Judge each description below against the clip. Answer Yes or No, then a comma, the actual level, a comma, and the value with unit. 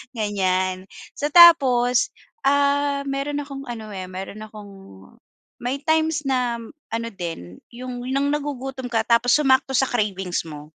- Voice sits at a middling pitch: No, high, 245 Hz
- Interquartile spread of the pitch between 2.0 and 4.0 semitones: No, average, 5.3 semitones